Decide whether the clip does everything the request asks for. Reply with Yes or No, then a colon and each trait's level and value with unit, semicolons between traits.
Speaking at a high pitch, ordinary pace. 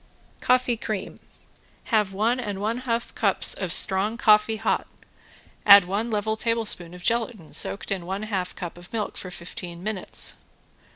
Yes: high, 210 Hz; average, 155 wpm